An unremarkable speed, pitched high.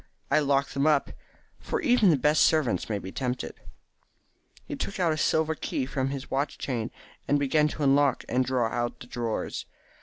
No: average, 180 wpm; medium, 140 Hz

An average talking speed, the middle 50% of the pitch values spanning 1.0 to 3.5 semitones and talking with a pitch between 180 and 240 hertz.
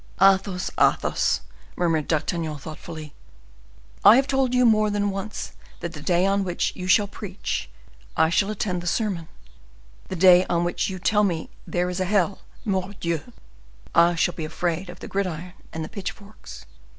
Yes: average, 170 wpm; average, 3.1 semitones; medium, 185 Hz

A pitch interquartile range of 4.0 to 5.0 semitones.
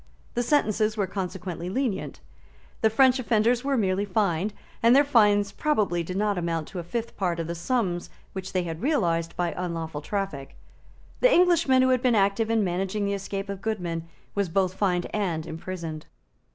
Yes: average, 4.4 semitones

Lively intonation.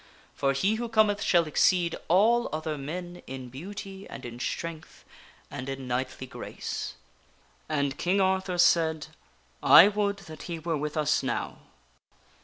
Yes: wide, 5.7 semitones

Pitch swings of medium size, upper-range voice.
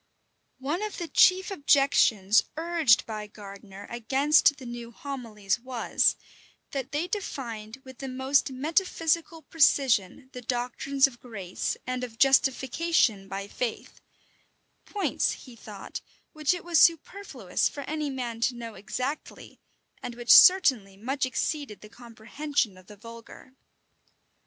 Yes: average, 4.5 semitones; very high, 255 Hz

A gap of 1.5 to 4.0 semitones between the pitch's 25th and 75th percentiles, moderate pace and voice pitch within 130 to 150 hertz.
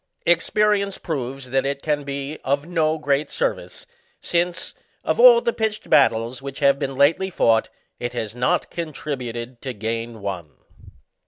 No: wide, 5.5 semitones; average, 155 wpm; medium, 140 Hz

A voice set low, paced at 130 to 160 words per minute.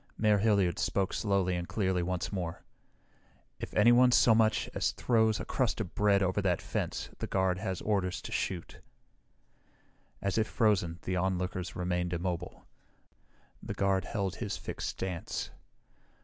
Yes: very low, 95 Hz; average, 150 wpm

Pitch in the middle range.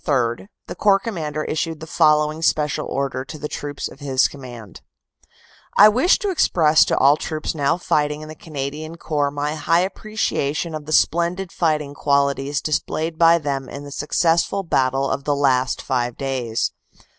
Yes: medium, 150 Hz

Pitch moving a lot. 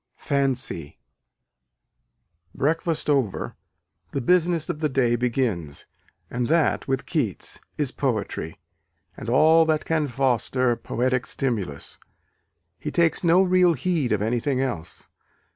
No: average, 4.8 semitones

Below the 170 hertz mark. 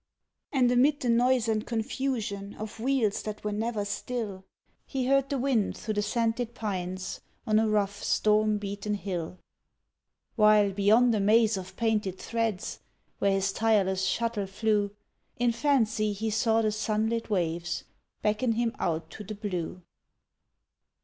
No: high, 215 Hz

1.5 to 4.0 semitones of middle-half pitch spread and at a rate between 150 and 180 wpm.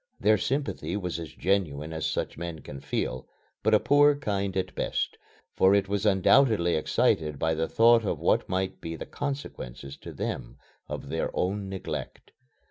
No: average, 4.9 semitones; average, 170 wpm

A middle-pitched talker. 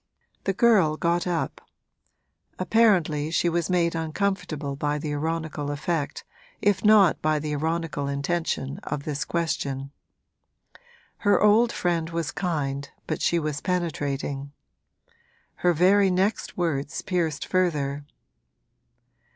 Yes: medium, 165 Hz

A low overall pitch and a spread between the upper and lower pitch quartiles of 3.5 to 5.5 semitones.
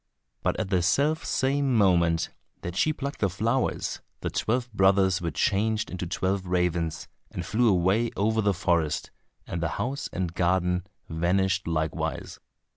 Yes: very low, 95 Hz; average, 4.2 semitones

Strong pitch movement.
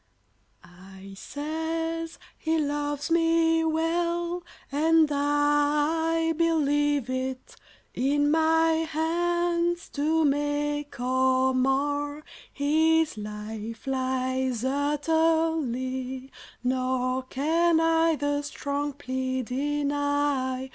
No: average, 3.7 semitones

